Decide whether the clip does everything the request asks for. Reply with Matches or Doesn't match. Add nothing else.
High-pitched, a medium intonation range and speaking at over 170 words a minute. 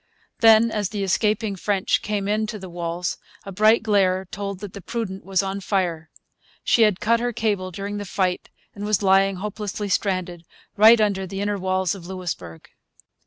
Doesn't match